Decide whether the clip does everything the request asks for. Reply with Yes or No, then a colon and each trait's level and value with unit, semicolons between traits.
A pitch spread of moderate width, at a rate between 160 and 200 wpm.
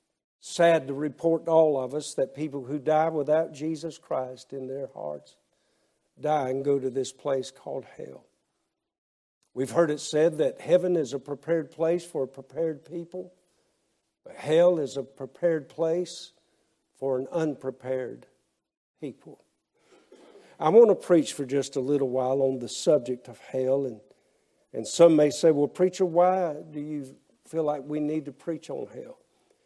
Yes: average, 4.0 semitones; average, 165 wpm